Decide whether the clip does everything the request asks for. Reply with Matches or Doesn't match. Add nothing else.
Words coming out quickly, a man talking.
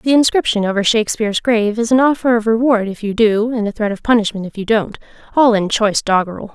Doesn't match